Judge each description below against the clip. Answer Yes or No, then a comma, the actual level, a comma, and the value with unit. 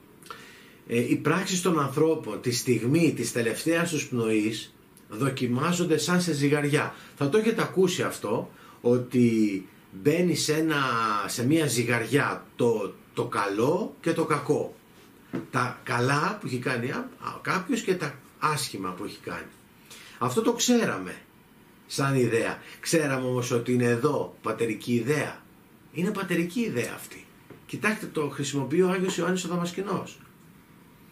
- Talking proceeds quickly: No, average, 135 wpm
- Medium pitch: Yes, medium, 150 Hz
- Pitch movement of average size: No, wide, 6.0 semitones